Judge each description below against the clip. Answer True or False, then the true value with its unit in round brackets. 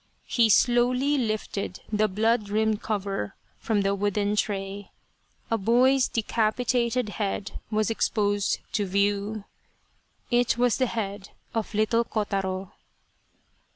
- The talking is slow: True (115 wpm)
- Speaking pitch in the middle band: False (215 Hz)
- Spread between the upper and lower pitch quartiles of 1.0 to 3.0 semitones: True (2.6 semitones)